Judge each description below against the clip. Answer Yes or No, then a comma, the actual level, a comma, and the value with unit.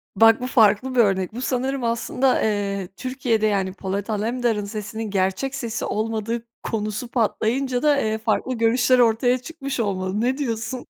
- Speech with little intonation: No, average, 3.3 semitones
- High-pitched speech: Yes, high, 225 Hz